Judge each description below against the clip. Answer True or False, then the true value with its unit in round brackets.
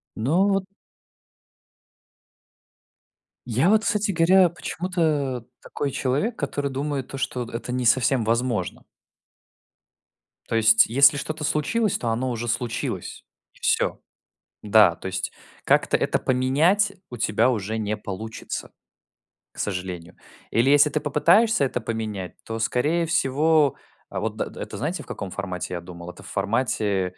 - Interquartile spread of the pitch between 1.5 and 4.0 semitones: False (5.5 semitones)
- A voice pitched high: False (130 Hz)